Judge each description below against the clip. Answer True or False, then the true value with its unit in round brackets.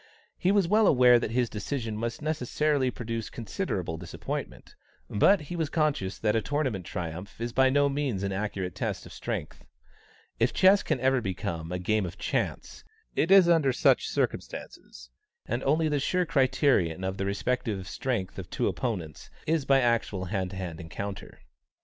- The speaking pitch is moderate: False (120 Hz)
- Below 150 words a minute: False (170 wpm)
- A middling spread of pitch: False (7.1 semitones)